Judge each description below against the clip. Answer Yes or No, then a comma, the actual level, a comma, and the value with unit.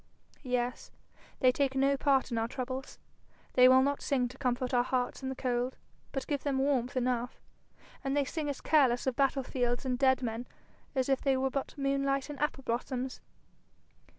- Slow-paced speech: No, average, 185 wpm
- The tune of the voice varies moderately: No, narrow, 1.6 semitones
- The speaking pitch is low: No, very high, 260 Hz